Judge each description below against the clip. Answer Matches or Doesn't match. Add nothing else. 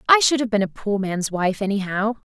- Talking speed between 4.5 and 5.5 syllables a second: Matches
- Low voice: Doesn't match